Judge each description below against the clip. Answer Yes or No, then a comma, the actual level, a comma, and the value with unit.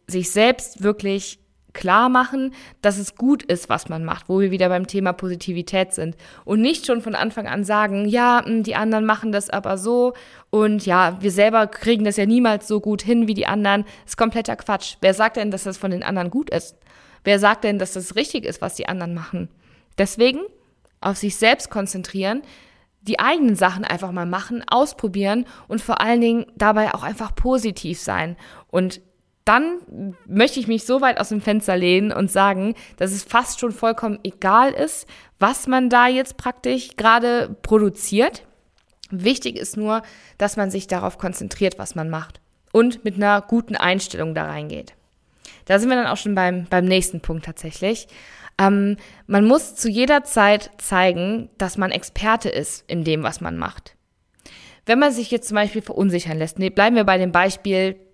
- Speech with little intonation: No, average, 3.6 semitones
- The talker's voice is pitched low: No, high, 205 Hz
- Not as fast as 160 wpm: No, average, 185 wpm